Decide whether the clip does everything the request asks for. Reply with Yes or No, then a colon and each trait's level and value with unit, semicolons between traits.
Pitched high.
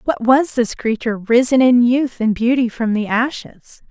Yes: high, 240 Hz